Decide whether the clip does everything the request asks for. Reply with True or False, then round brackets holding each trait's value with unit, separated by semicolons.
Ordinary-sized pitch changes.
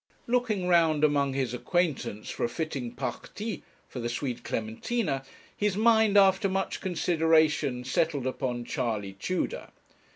False (7.3 semitones)